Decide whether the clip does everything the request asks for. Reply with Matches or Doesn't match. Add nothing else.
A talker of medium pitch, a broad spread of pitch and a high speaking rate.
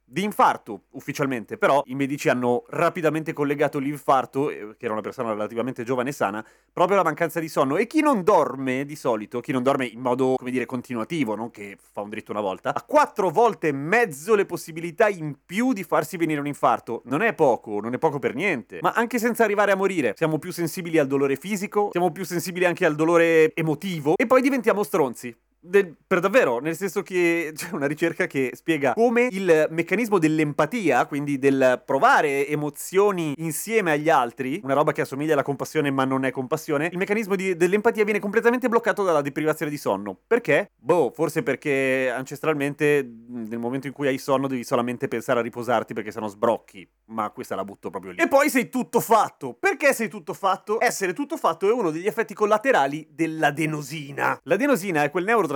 Matches